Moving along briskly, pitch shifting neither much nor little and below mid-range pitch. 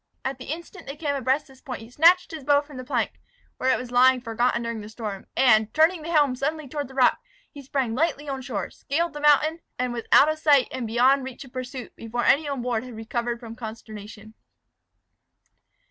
No: fast, 215 wpm; average, 3.5 semitones; very high, 260 Hz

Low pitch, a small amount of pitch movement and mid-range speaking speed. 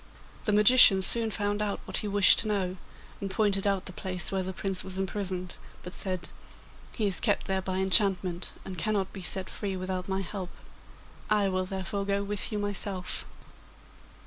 No: high, 195 Hz; narrow, 1.6 semitones; average, 180 wpm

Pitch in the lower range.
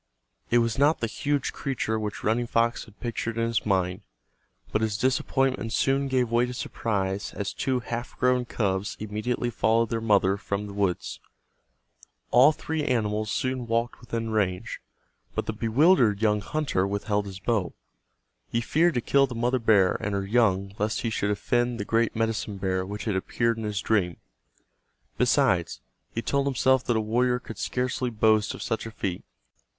Yes: low, 115 Hz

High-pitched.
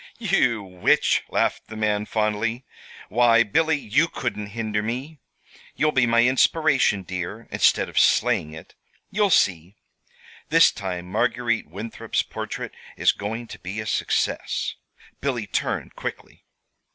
No: low, 115 Hz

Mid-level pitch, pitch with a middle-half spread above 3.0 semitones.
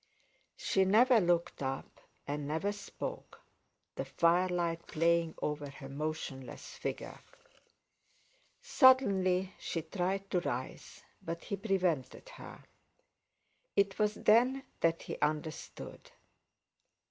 Yes: medium, 175 Hz; average, 4.3 semitones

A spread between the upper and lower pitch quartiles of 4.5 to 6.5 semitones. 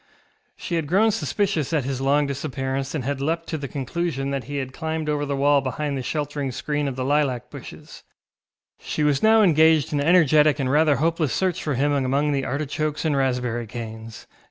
No: narrow, 2.6 semitones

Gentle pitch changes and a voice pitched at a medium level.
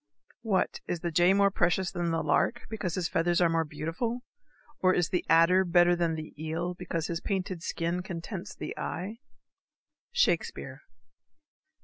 Yes: narrow, 2.2 semitones; medium, 175 Hz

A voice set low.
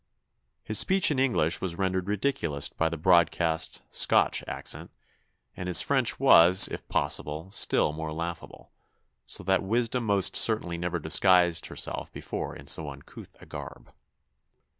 Yes: very low, 90 Hz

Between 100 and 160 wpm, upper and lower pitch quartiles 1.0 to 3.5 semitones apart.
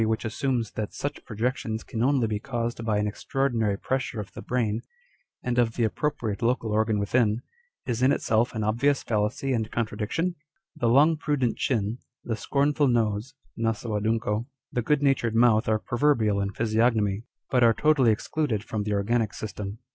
No: average, 175 wpm; average, 2.9 semitones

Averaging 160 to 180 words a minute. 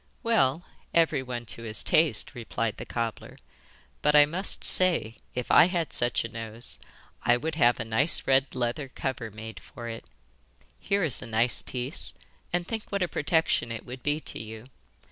Yes: average, 175 wpm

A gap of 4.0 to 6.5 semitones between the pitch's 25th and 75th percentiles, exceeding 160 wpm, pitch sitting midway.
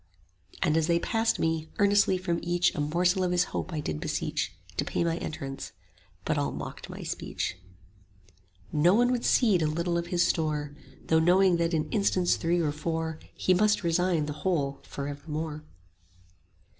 No: average, 3.0 semitones; average, 180 wpm; medium, 170 Hz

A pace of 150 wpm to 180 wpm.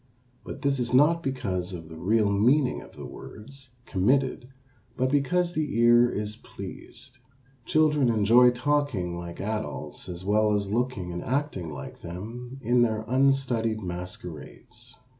No: average, 140 wpm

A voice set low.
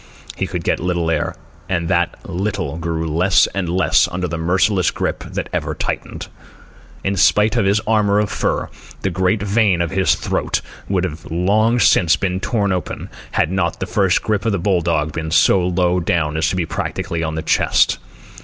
Yes: very low, 90 Hz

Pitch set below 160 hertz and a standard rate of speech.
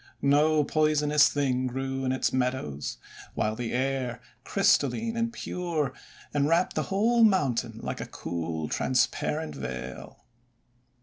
No: low, 135 Hz; slow, 125 wpm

